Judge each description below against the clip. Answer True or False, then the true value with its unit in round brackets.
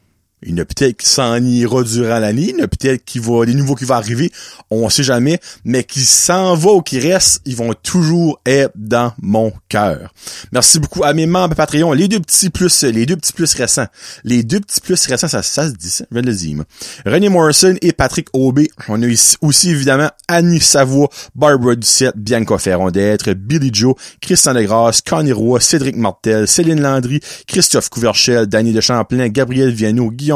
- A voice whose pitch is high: False (130 Hz)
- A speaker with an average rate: True (190 wpm)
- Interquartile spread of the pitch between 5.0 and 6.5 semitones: True (5.3 semitones)